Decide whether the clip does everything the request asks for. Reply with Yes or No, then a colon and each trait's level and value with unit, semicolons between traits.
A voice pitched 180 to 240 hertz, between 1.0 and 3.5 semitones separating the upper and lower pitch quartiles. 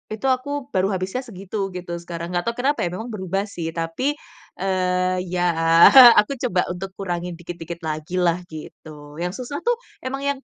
No: medium, 185 Hz; average, 4.2 semitones